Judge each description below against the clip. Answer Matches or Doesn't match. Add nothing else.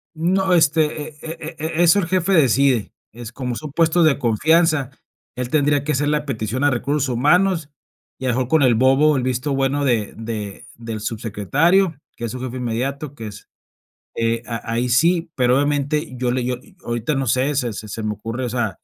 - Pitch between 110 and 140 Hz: Matches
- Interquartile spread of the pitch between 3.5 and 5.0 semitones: Matches